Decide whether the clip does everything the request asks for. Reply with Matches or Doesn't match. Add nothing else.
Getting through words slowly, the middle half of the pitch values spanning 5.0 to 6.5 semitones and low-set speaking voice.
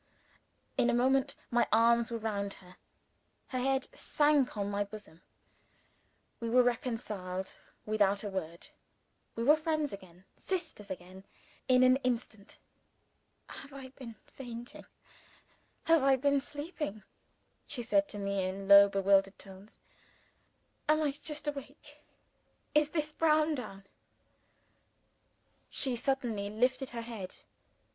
Doesn't match